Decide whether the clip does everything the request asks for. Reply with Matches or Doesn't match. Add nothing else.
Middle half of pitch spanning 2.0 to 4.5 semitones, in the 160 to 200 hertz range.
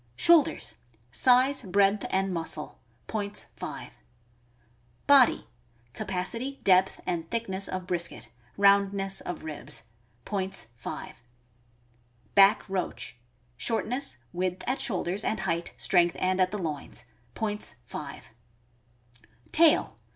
Matches